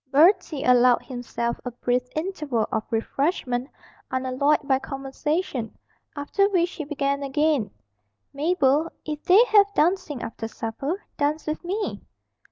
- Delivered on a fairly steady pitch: No, average, 4.5 semitones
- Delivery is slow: Yes, slow, 125 wpm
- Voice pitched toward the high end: Yes, very high, 285 Hz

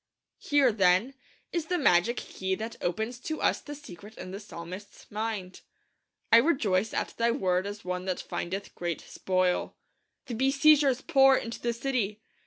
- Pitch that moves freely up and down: Yes, wide, 6.3 semitones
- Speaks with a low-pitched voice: No, high, 220 Hz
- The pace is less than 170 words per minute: Yes, average, 160 wpm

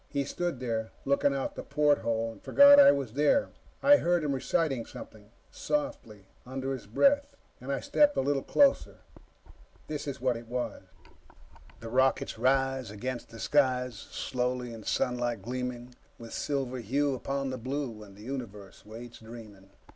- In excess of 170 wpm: No, average, 160 wpm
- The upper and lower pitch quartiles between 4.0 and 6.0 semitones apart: No, average, 3.4 semitones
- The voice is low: Yes, low, 130 Hz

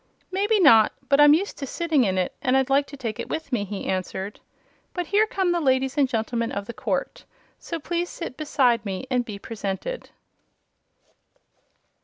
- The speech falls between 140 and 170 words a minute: No, average, 185 wpm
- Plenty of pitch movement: Yes, wide, 7.1 semitones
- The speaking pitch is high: Yes, very high, 265 Hz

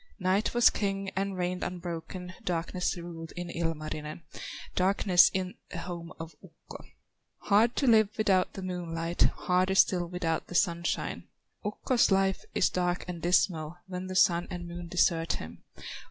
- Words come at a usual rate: Yes, average, 150 wpm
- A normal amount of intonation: No, narrow, 2.0 semitones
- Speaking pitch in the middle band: Yes, medium, 180 Hz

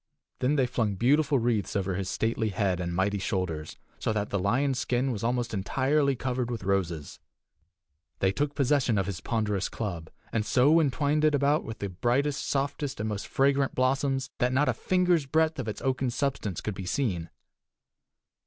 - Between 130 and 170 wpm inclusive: No, average, 180 wpm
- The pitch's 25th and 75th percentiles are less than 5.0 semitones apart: No, wide, 5.6 semitones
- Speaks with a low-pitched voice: Yes, low, 120 Hz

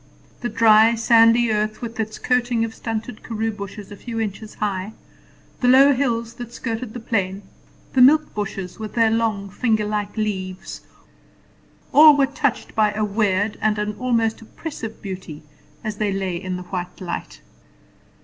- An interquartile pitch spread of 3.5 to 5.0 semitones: No, narrow, 2.4 semitones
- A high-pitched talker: Yes, high, 220 Hz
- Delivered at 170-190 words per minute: No, average, 160 wpm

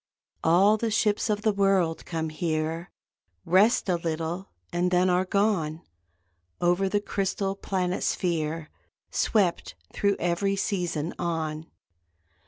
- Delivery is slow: Yes, slow, 120 wpm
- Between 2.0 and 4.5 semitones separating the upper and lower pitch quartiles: Yes, average, 3.2 semitones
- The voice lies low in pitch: No, medium, 180 Hz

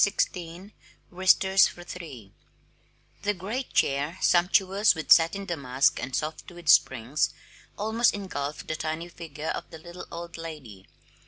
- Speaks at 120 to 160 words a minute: Yes, average, 145 wpm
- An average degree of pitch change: Yes, average, 3.9 semitones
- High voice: No, medium, 170 Hz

